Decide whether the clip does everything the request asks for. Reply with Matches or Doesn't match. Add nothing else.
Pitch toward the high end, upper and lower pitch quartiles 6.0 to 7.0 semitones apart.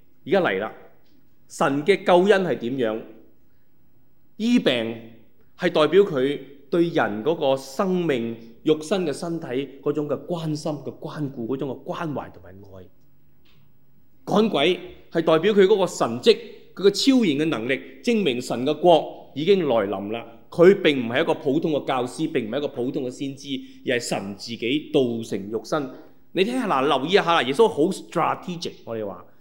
Doesn't match